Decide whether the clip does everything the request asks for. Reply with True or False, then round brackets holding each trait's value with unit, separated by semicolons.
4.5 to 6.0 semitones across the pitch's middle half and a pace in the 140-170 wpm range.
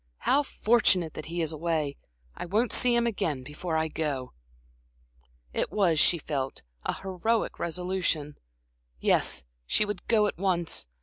True (5.0 semitones; 145 wpm)